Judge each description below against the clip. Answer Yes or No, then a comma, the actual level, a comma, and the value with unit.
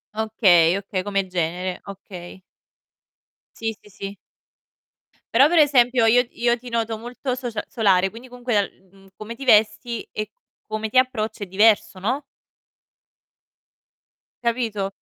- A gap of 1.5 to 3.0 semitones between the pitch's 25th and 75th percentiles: No, average, 3.6 semitones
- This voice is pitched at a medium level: No, high, 220 Hz